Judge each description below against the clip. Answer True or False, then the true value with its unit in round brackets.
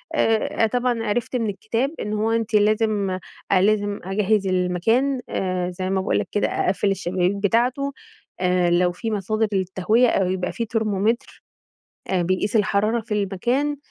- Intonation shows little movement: False (3.3 semitones)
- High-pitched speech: True (210 Hz)